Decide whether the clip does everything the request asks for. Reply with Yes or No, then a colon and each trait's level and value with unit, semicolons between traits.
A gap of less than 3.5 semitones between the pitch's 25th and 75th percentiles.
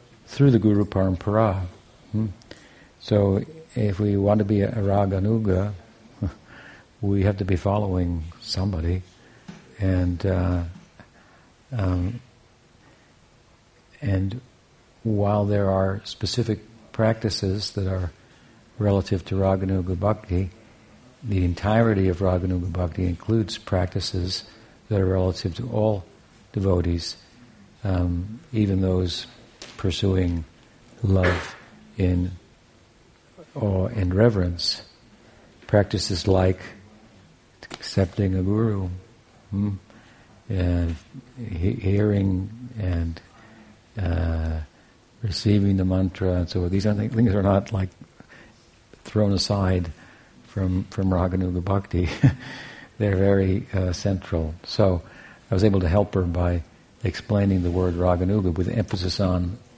Yes: average, 3.0 semitones